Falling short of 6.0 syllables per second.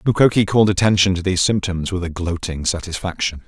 No: 6.3 syllables/s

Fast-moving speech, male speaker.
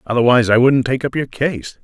Yes: fast, 230 wpm; male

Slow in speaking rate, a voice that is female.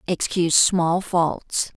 Yes: slow, 100 wpm; female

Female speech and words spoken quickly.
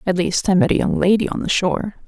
Yes: female; fast, 290 wpm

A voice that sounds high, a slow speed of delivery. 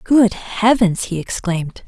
Yes: high, 200 Hz; slow, 130 wpm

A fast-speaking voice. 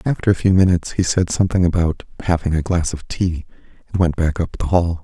Yes: fast, 225 wpm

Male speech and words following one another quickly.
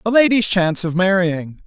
No: male; average, 180 wpm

